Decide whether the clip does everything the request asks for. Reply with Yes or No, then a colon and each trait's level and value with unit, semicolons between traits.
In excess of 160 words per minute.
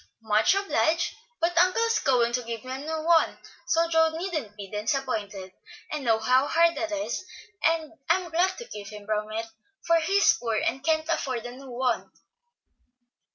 Yes: average, 180 wpm